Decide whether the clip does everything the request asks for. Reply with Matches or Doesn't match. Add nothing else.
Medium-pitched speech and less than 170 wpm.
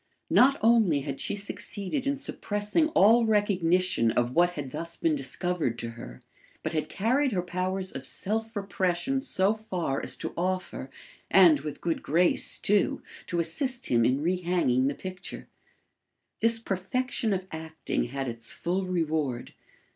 Matches